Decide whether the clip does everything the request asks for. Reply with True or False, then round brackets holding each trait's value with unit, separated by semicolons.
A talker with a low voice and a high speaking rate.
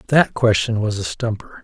False (110 Hz; 185 wpm)